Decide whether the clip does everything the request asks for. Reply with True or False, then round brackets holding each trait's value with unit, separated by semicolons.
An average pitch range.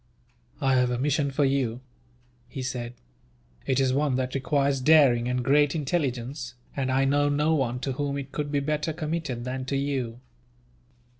False (2.3 semitones)